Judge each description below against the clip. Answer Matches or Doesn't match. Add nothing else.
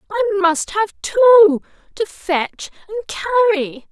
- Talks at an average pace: Doesn't match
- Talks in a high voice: Matches